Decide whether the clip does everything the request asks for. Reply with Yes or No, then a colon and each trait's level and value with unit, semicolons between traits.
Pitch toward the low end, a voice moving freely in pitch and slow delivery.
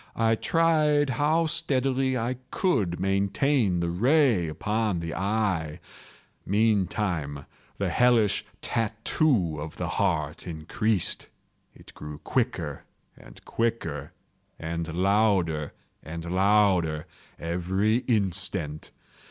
Yes: low, 100 Hz; wide, 5.7 semitones; slow, 95 wpm